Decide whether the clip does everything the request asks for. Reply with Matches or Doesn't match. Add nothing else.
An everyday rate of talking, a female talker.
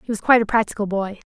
Doesn't match